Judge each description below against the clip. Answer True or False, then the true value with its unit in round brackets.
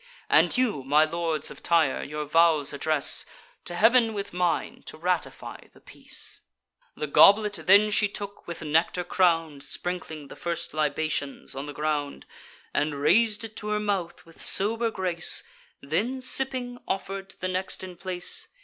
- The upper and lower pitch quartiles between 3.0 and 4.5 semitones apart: False (4.9 semitones)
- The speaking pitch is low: False (175 Hz)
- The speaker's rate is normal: True (160 wpm)